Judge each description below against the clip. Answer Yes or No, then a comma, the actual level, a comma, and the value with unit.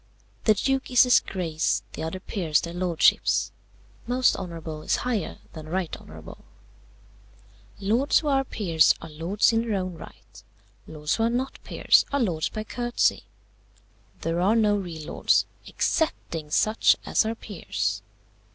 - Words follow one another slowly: No, average, 150 wpm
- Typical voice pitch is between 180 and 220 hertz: Yes, high, 190 Hz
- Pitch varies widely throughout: Yes, wide, 6.0 semitones